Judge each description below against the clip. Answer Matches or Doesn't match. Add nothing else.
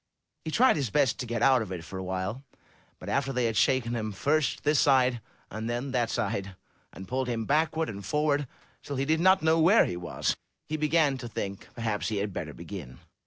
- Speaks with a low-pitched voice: Matches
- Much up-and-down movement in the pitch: Matches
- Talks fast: Matches